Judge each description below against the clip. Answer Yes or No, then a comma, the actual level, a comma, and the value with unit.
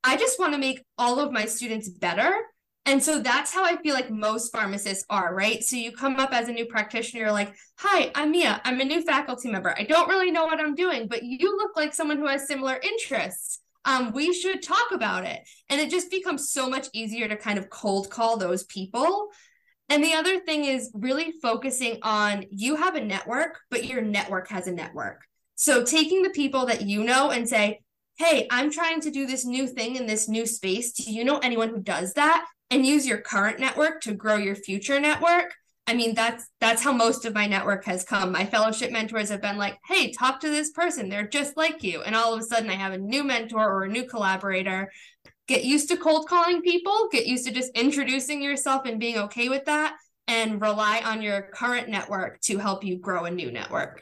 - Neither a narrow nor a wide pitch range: No, wide, 5.9 semitones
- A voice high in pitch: Yes, high, 245 Hz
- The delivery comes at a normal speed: No, fast, 225 wpm